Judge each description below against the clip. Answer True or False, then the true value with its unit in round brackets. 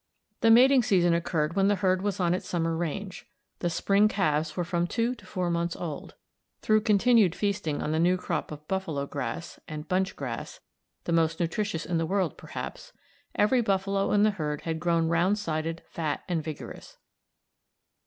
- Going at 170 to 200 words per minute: True (180 wpm)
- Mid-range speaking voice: True (175 Hz)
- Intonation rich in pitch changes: False (3.6 semitones)